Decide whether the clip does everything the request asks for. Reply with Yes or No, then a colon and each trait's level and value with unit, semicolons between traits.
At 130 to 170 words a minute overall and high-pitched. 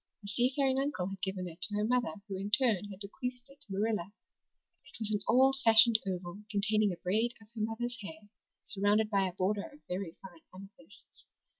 No: average, 195 wpm; high, 210 Hz